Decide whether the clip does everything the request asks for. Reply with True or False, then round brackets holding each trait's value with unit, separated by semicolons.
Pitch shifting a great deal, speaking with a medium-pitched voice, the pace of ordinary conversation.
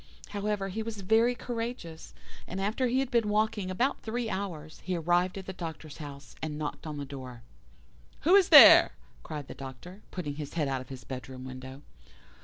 True (7.0 semitones; 180 Hz; 190 wpm)